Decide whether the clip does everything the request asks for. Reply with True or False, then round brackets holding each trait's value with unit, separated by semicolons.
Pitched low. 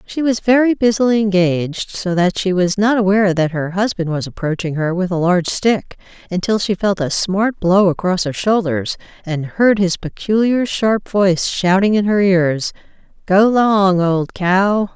False (190 Hz)